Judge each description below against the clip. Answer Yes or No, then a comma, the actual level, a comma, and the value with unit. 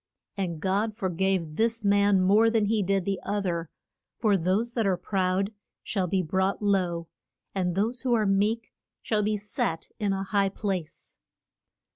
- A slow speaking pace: No, average, 170 wpm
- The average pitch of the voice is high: Yes, high, 195 Hz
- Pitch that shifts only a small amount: Yes, narrow, 2.3 semitones